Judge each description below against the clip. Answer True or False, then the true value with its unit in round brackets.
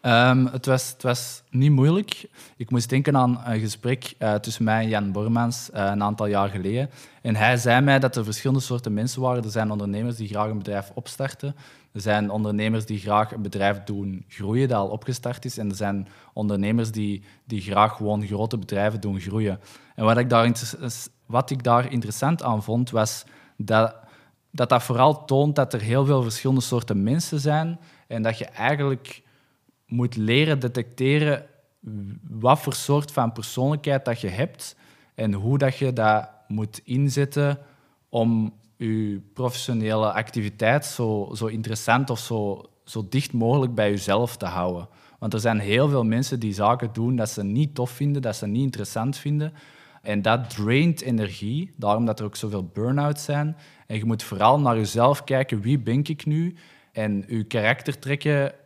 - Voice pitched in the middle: False (120 Hz)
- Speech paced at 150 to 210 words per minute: True (180 wpm)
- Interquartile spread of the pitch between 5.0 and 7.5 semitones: False (4.0 semitones)